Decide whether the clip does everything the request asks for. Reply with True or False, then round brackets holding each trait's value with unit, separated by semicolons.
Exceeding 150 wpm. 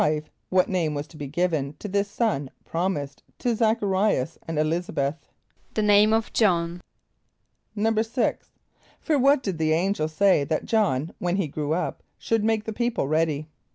True (180 wpm)